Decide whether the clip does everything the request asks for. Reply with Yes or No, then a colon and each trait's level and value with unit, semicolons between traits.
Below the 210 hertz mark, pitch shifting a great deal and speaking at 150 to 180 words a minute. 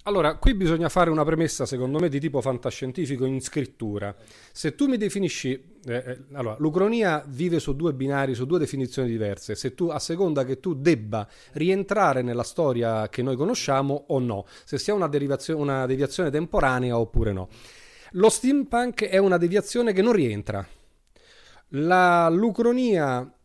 Yes: medium, 140 Hz; wide, 6.0 semitones; average, 160 wpm